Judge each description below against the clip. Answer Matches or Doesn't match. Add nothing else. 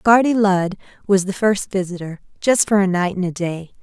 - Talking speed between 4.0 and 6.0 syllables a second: Matches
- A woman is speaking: Matches